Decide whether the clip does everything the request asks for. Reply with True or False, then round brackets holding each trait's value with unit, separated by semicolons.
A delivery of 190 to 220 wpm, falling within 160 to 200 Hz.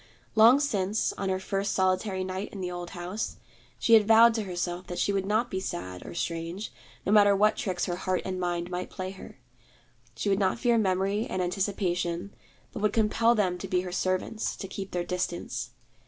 True (200 wpm; 190 Hz)